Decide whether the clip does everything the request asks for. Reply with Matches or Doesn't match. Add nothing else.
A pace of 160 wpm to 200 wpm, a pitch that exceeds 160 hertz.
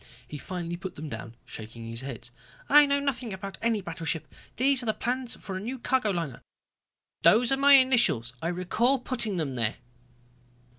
Matches